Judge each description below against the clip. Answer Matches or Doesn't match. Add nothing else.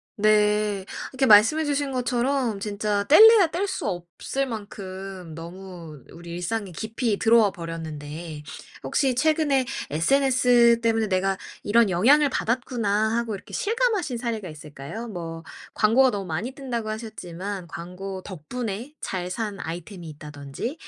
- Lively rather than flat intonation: Matches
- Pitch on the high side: Matches